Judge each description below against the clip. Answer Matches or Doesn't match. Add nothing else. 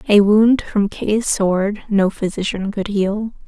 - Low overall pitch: Doesn't match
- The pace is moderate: Matches